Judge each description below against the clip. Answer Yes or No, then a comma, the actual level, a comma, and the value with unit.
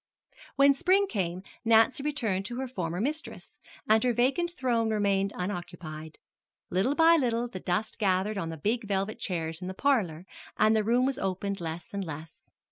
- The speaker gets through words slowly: No, average, 175 wpm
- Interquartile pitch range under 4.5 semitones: No, wide, 5.6 semitones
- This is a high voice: Yes, high, 210 Hz